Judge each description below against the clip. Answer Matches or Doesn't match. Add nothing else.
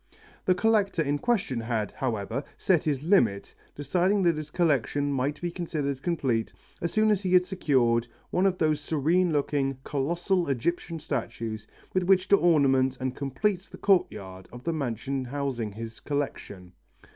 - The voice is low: Doesn't match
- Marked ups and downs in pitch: Matches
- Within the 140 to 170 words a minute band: Matches